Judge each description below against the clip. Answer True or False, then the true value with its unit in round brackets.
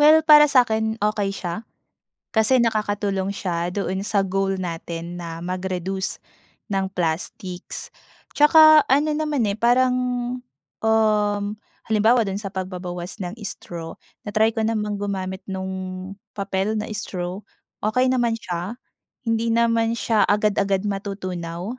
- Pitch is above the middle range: True (205 Hz)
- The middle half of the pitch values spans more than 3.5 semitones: False (3.2 semitones)